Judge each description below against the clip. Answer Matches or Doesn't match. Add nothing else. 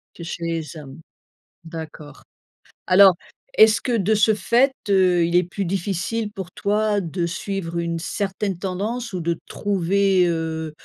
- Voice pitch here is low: Doesn't match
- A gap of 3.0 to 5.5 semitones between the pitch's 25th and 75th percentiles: Matches